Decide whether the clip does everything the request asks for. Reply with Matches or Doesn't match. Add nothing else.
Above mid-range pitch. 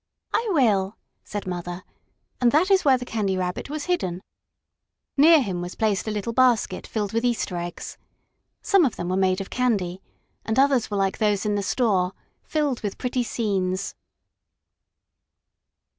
Matches